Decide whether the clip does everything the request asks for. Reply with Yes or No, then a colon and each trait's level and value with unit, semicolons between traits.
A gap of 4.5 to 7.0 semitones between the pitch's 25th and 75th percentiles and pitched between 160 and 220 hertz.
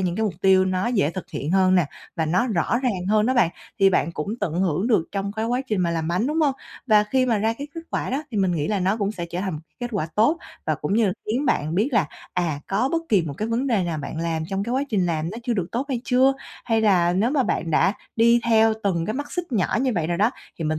Yes: average, 5.2 semitones; high, 200 Hz